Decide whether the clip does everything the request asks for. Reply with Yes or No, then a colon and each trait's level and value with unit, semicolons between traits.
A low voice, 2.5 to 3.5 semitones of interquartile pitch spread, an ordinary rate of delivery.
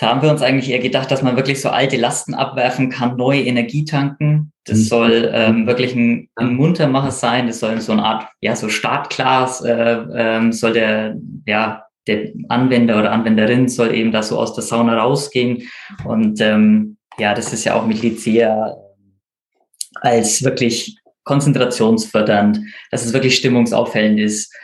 Yes: low, 120 Hz; average, 2.8 semitones; average, 170 wpm